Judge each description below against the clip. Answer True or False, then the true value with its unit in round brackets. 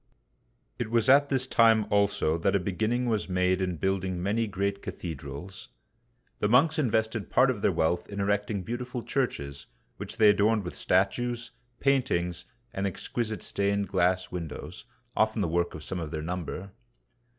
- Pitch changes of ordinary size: True (3.9 semitones)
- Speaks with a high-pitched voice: False (100 Hz)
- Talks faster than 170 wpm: False (160 wpm)